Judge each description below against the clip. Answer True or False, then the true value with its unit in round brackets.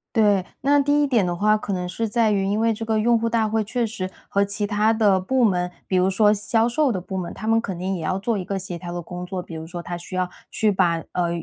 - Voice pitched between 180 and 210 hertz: True (200 Hz)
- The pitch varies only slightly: False (3.5 semitones)